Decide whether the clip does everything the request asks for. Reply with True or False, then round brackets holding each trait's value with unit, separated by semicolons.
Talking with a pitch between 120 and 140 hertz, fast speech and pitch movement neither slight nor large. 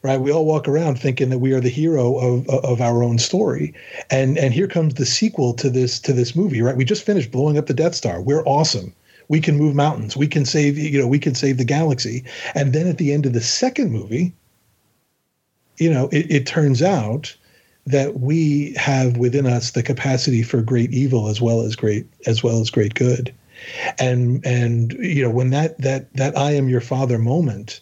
True (135 Hz; 215 wpm; 3.4 semitones)